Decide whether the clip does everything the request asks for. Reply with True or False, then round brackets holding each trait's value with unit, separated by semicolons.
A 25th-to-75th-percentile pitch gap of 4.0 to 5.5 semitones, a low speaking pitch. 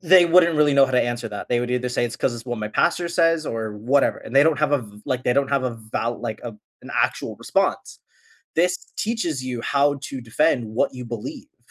True (4.4 semitones; 130 Hz)